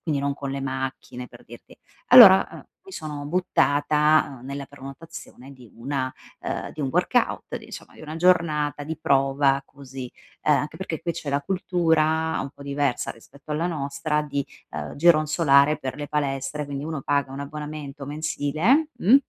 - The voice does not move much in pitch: Yes, narrow, 2.2 semitones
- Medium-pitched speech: Yes, medium, 145 Hz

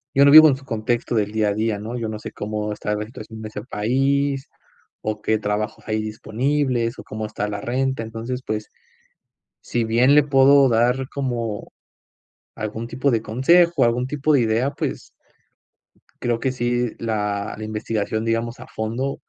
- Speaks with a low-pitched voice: Yes, low, 115 Hz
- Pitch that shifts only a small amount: No, average, 3.5 semitones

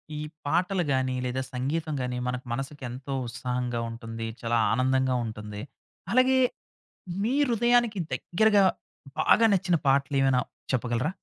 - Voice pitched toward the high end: No, low, 130 Hz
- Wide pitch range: Yes, wide, 6.3 semitones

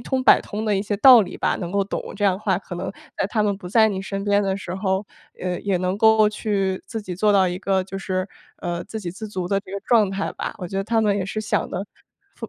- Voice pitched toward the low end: No, high, 195 Hz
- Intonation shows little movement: Yes, narrow, 2.0 semitones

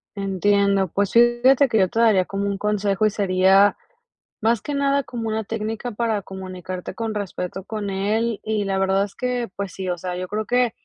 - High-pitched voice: Yes, high, 205 Hz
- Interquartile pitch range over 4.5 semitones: No, average, 2.8 semitones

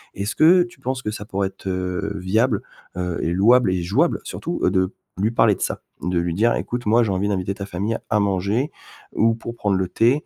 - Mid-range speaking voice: No, low, 100 Hz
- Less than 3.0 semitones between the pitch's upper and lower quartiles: No, average, 4.0 semitones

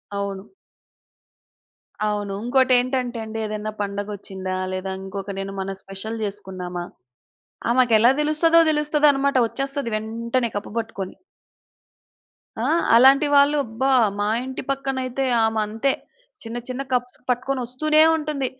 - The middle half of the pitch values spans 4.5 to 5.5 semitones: Yes, average, 4.8 semitones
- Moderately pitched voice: No, high, 235 Hz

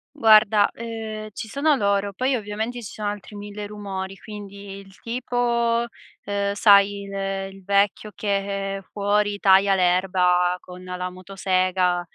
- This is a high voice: Yes, high, 200 Hz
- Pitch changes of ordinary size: No, narrow, 1.8 semitones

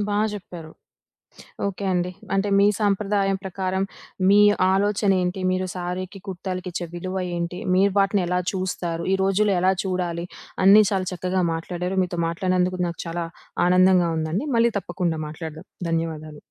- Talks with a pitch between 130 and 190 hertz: Yes, medium, 185 Hz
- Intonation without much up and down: Yes, narrow, 1.9 semitones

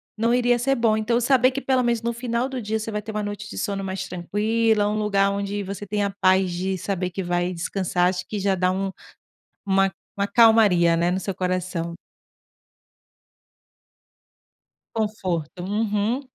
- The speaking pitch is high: Yes, high, 200 Hz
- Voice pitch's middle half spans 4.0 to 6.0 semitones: No, average, 3.2 semitones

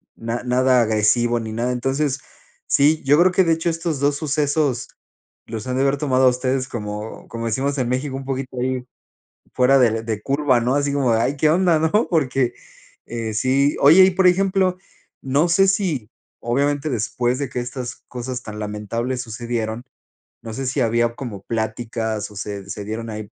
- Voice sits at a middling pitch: No, low, 130 Hz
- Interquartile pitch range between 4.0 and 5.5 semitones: No, average, 3.6 semitones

